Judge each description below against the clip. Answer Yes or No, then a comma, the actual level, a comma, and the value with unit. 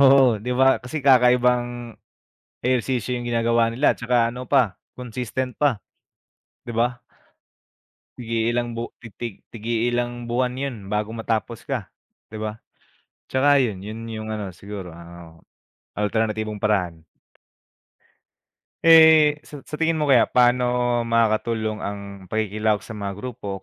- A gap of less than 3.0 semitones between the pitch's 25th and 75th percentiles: Yes, narrow, 2.6 semitones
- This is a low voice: Yes, low, 120 Hz